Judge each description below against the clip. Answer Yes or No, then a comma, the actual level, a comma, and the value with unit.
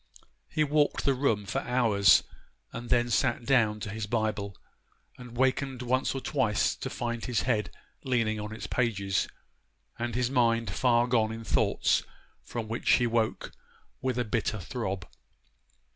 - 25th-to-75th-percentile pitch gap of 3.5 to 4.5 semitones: No, narrow, 2.6 semitones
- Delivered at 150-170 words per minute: Yes, average, 155 wpm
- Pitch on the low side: Yes, low, 120 Hz